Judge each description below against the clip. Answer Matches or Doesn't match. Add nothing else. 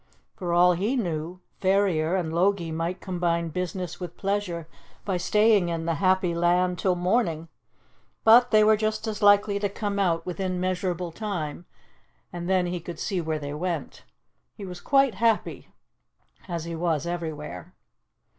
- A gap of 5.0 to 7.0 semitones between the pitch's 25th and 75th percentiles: Doesn't match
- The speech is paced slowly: Doesn't match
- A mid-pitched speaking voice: Matches